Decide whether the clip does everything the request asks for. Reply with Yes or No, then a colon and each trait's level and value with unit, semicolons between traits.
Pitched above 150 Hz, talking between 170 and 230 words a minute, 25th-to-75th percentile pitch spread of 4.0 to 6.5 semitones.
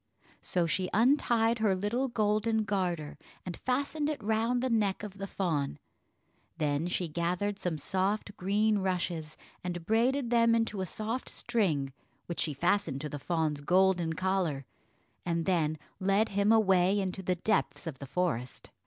No: high, 190 Hz; average, 155 wpm; average, 4.4 semitones